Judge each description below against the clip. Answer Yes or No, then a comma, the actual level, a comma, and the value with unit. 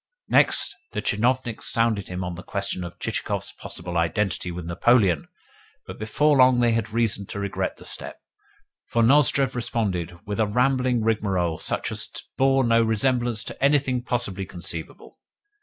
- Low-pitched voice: Yes, low, 110 Hz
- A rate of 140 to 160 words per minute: Yes, average, 155 wpm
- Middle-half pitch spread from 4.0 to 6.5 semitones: Yes, average, 4.9 semitones